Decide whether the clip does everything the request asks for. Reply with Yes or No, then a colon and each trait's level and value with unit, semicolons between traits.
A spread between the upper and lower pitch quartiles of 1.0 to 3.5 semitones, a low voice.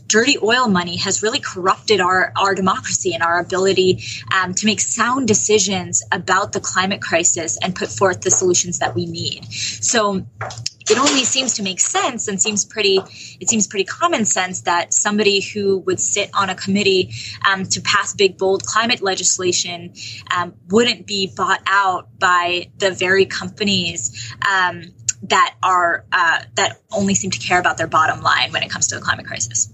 No: average, 3.0 semitones; high, 190 Hz